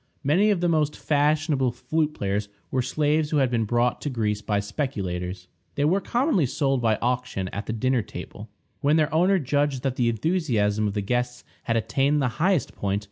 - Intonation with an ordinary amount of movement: No, wide, 5.7 semitones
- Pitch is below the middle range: Yes, low, 130 Hz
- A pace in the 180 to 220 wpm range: Yes, average, 190 wpm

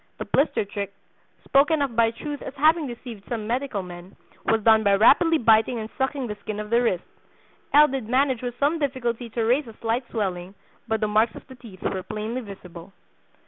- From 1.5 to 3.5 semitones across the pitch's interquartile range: No, average, 4.0 semitones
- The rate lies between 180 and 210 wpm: Yes, average, 200 wpm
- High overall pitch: Yes, high, 230 Hz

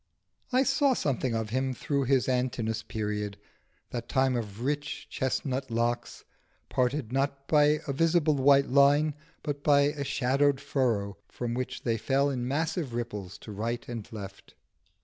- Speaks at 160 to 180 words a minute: No, average, 150 wpm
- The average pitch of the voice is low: Yes, low, 130 Hz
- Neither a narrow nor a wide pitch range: Yes, average, 3.5 semitones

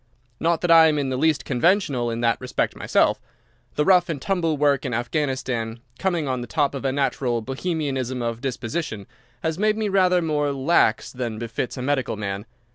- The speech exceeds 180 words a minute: Yes, average, 190 wpm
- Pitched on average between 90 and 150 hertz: Yes, medium, 140 Hz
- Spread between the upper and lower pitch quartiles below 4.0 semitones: No, average, 4.9 semitones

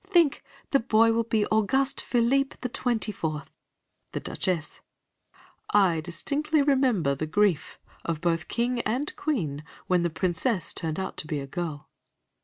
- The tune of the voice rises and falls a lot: Yes, wide, 7.5 semitones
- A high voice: Yes, high, 205 Hz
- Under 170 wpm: Yes, average, 155 wpm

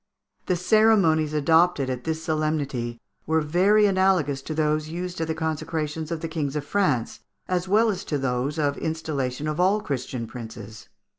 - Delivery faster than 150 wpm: Yes, average, 165 wpm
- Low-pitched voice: No, medium, 155 Hz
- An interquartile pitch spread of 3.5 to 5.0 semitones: Yes, average, 3.9 semitones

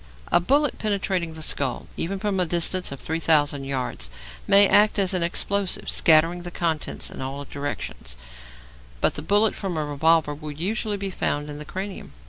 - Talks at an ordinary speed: Yes, average, 175 wpm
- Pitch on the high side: No, medium, 170 Hz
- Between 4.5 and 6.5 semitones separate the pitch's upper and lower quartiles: Yes, average, 5.0 semitones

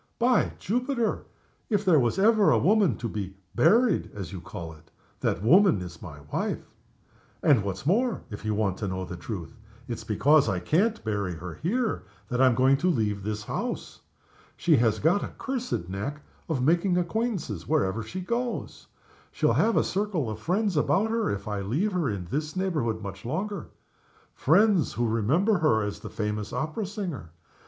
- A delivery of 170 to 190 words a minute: Yes, average, 175 wpm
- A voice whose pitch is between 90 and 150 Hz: Yes, medium, 140 Hz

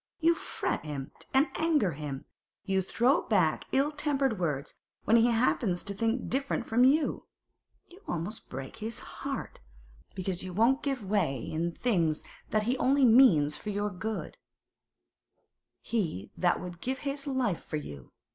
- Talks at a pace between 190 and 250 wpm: No, average, 155 wpm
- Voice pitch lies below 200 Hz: No, high, 215 Hz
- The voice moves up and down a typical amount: No, wide, 7.4 semitones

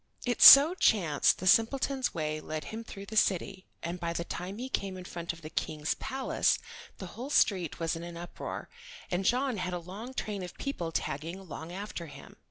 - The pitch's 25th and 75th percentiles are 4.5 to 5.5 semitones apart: Yes, average, 4.9 semitones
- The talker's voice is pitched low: No, medium, 185 Hz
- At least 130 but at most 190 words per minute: No, average, 200 wpm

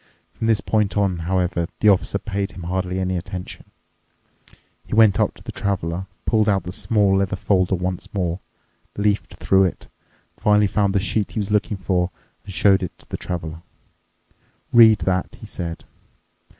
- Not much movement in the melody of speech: Yes, narrow, 2.3 semitones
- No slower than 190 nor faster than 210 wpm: No, average, 170 wpm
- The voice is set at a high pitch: No, very low, 95 Hz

